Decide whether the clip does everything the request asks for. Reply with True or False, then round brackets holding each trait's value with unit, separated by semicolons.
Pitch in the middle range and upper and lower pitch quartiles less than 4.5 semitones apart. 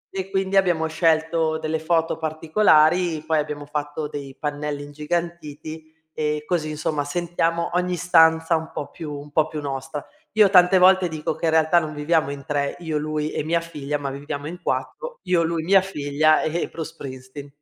True (155 Hz; 2.4 semitones)